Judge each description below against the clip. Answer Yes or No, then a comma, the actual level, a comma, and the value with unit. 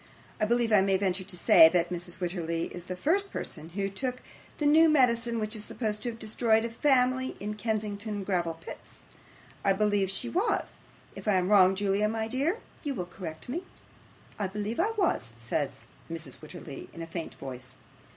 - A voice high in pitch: Yes, high, 205 Hz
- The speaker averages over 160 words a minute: Yes, average, 190 wpm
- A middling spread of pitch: Yes, average, 4.8 semitones